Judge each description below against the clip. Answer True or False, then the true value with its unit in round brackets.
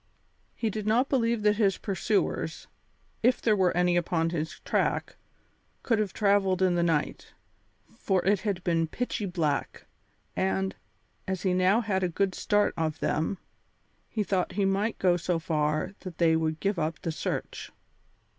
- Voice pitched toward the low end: False (190 Hz)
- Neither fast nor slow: True (165 wpm)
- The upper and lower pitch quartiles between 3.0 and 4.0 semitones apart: True (3.5 semitones)